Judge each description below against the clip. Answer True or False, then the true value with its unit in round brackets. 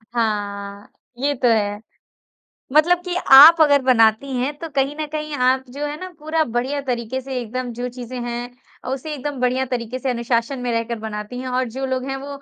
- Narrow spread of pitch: False (3.0 semitones)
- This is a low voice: False (255 Hz)